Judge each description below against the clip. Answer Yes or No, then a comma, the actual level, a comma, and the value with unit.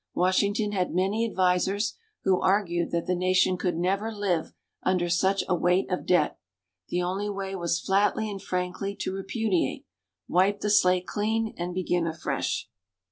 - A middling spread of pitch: No, narrow, 2.1 semitones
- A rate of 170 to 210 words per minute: No, average, 155 wpm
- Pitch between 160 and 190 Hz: Yes, medium, 185 Hz